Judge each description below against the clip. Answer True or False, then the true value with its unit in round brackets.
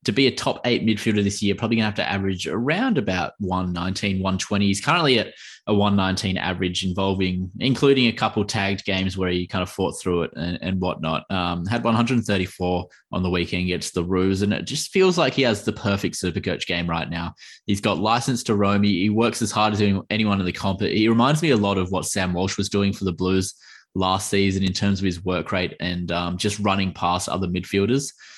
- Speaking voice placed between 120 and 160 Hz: False (95 Hz)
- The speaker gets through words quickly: True (225 wpm)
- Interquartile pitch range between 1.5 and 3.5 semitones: True (2.5 semitones)